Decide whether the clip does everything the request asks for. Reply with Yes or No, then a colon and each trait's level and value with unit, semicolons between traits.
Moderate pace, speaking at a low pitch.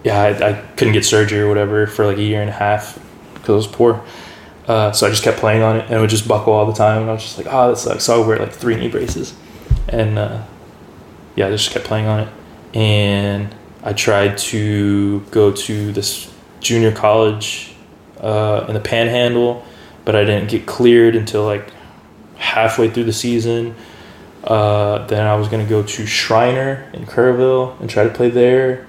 No: fast, 210 wpm; low, 110 Hz